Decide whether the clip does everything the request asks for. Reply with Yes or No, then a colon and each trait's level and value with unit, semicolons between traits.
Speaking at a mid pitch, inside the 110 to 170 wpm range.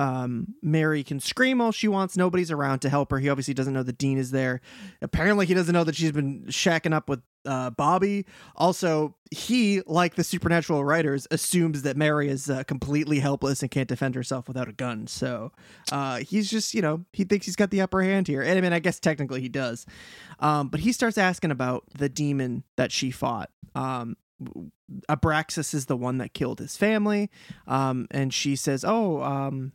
No: medium, 150 Hz; average, 200 wpm